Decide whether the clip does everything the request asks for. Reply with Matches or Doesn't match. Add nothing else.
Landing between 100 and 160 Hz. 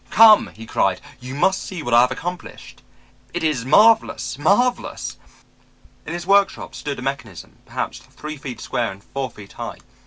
Matches